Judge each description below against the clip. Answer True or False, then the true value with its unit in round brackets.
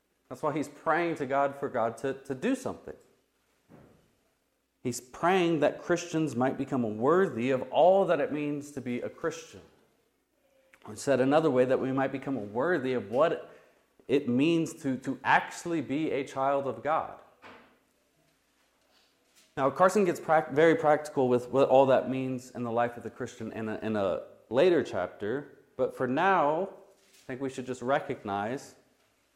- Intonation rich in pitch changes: False (4.0 semitones)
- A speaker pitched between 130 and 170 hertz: True (135 Hz)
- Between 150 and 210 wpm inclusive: True (165 wpm)